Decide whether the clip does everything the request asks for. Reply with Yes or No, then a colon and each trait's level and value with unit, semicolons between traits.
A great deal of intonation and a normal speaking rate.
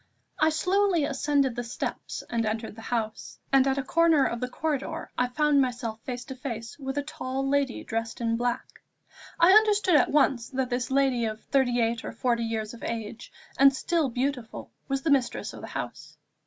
No: average, 3.4 semitones; average, 195 wpm